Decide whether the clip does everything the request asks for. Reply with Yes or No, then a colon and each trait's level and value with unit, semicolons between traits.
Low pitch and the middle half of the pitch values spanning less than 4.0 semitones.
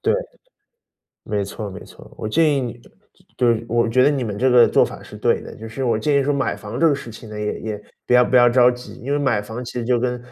Yes: low, 120 Hz; average, 2.8 semitones